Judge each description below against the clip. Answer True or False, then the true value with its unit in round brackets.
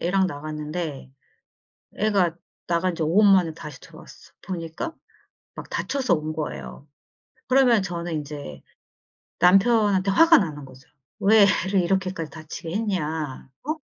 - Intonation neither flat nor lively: True (4.2 semitones)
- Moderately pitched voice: True (175 Hz)